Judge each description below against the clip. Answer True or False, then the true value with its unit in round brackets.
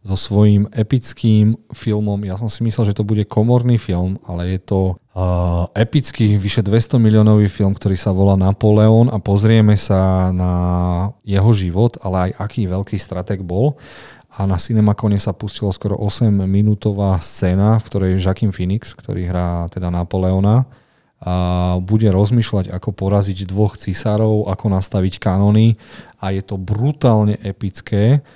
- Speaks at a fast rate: False (150 wpm)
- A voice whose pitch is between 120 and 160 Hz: False (100 Hz)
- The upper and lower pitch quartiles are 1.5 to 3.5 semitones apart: True (2.5 semitones)